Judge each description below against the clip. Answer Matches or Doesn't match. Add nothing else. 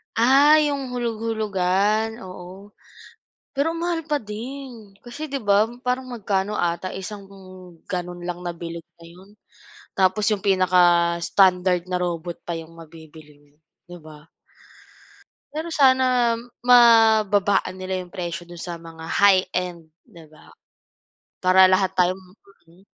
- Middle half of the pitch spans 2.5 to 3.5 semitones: Doesn't match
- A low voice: Doesn't match